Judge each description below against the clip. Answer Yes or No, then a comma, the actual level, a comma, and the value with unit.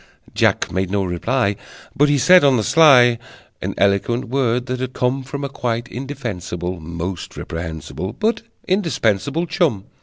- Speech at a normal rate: Yes, average, 150 wpm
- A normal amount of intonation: No, wide, 6.3 semitones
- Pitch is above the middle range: No, low, 120 Hz